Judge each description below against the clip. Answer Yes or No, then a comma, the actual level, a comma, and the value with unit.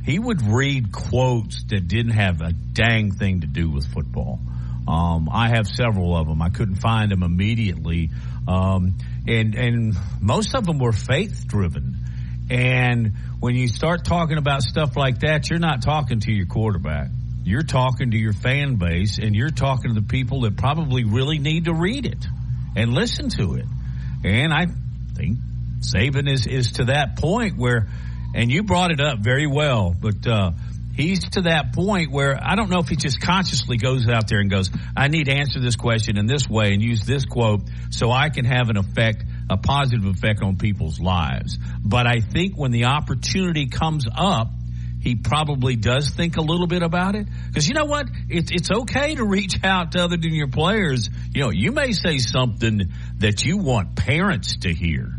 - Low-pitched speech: Yes, low, 115 Hz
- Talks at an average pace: Yes, average, 190 wpm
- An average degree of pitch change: No, wide, 6.5 semitones